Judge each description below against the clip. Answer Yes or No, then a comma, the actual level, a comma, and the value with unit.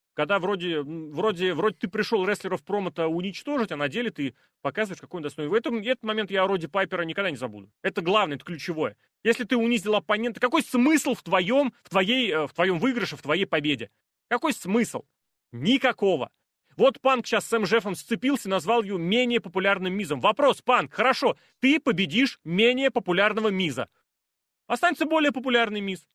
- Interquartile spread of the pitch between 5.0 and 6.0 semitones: Yes, average, 5.3 semitones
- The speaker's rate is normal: No, fast, 170 wpm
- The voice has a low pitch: No, high, 205 Hz